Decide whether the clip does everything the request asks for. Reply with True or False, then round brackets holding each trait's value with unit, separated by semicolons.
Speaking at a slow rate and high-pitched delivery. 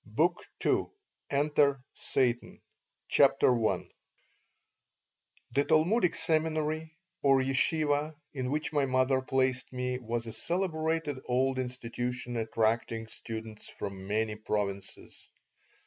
False (100 wpm; 130 Hz)